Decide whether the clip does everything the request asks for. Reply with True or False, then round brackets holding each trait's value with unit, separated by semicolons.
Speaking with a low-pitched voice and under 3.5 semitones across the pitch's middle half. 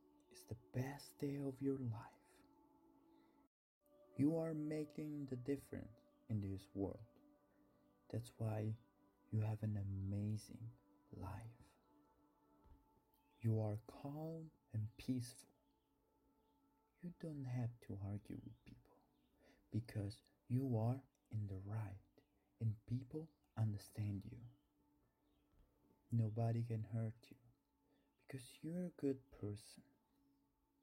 False (120 Hz; 5.4 semitones)